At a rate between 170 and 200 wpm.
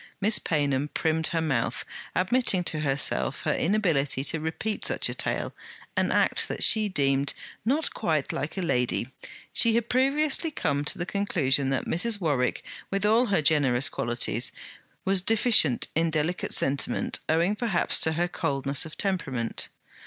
No: average, 155 wpm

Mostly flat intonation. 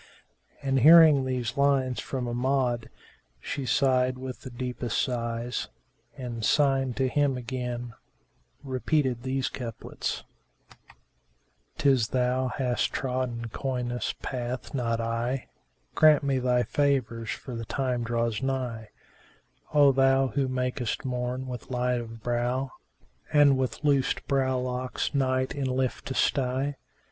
Yes: narrow, 1.7 semitones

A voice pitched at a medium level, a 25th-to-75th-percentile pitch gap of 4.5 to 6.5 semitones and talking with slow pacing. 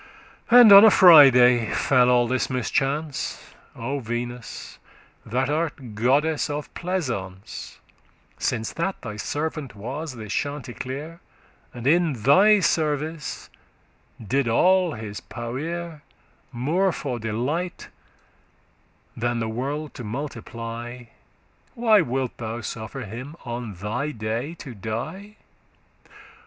No: low, 130 Hz; average, 5.1 semitones; slow, 110 wpm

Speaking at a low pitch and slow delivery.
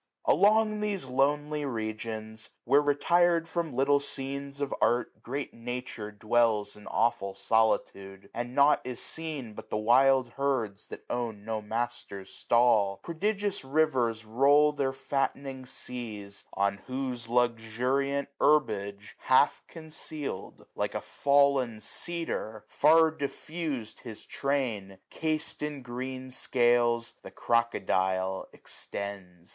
Yes: low, 125 Hz; slow, 120 wpm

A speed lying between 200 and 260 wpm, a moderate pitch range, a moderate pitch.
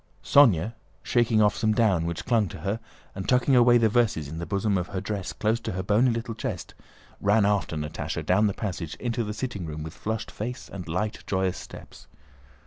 No: fast, 205 wpm; average, 3.8 semitones; low, 105 Hz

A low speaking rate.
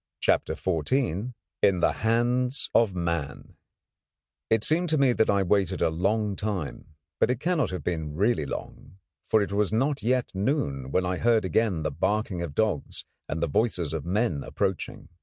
No: average, 175 wpm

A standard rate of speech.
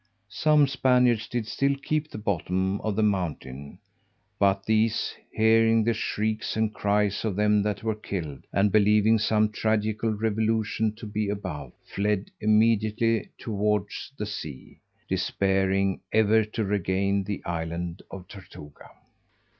No: slow, 130 wpm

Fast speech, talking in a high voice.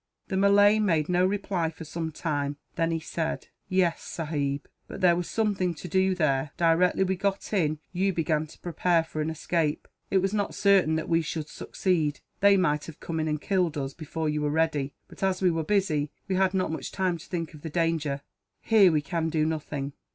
No: fast, 210 wpm; medium, 165 Hz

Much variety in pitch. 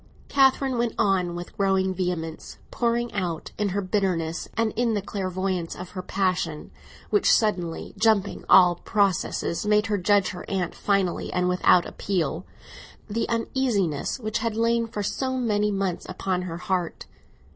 No: average, 3.3 semitones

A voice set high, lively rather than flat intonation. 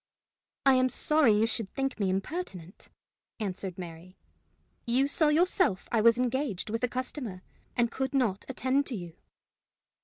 Yes: high, 235 Hz; wide, 5.7 semitones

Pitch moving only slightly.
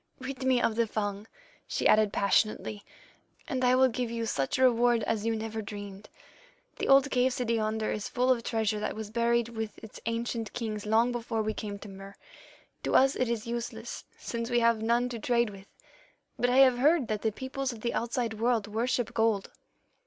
Yes: narrow, 2.2 semitones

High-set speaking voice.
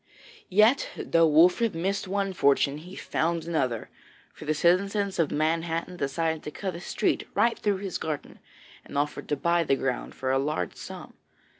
No: medium, 165 Hz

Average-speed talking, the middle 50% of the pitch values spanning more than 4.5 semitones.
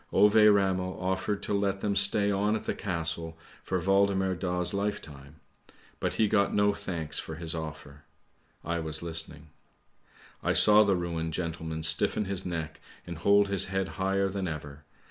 No: average, 165 wpm; average, 3.5 semitones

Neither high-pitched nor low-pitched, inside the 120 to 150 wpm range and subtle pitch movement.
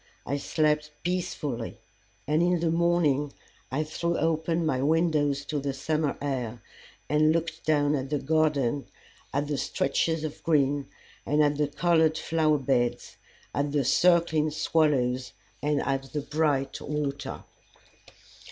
Yes: medium, 150 Hz; slow, 135 wpm; narrow, 2.3 semitones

